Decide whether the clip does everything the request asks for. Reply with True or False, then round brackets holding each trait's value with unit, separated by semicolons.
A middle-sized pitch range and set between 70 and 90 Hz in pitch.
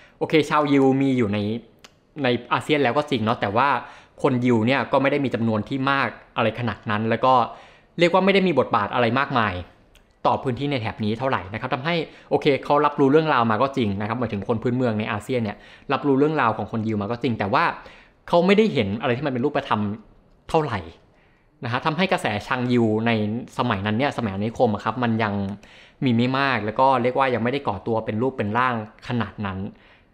False (4.2 semitones; 120 Hz)